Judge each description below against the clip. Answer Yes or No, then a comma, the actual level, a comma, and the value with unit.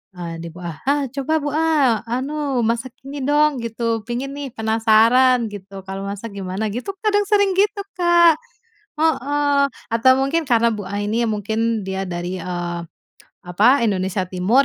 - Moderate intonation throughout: No, wide, 6.3 semitones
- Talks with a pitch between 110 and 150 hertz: No, high, 235 Hz